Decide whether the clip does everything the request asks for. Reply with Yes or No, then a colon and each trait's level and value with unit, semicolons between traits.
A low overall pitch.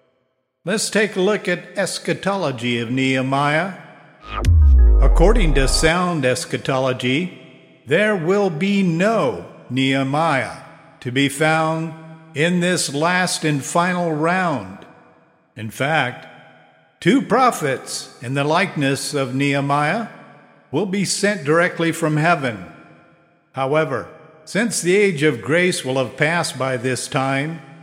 No: medium, 160 Hz